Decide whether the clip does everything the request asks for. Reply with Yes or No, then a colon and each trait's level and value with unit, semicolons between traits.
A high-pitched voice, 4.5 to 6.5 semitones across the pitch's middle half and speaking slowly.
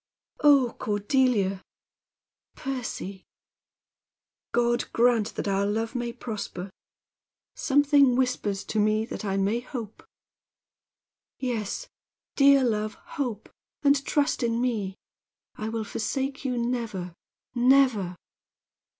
No: high, 235 Hz; average, 3.8 semitones; slow, 100 wpm